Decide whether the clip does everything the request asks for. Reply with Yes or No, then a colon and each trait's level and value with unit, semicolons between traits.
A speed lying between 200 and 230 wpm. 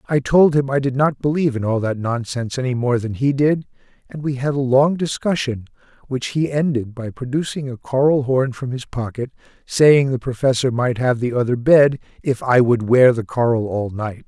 Yes: fast, 205 wpm